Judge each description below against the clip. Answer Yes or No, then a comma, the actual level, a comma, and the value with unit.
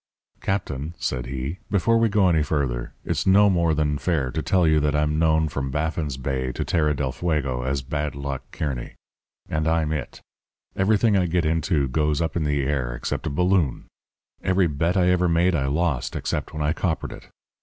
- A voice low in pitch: Yes, very low, 75 Hz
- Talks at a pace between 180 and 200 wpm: Yes, average, 195 wpm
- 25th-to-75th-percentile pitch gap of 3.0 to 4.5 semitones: Yes, average, 3.9 semitones